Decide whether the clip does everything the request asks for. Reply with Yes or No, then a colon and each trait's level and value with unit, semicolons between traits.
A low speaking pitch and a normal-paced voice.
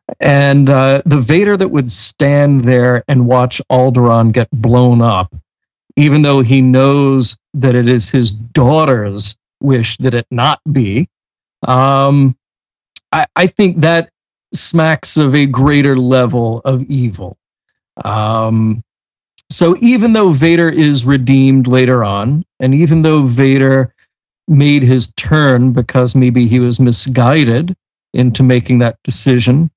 No: low, 130 Hz; slow, 130 wpm